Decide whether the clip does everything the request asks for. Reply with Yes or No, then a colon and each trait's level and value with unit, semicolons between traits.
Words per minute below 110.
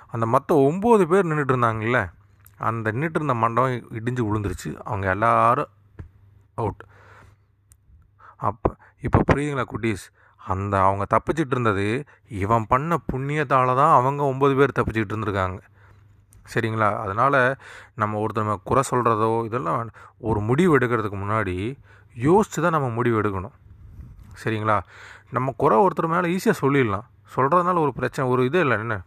No: average, 125 wpm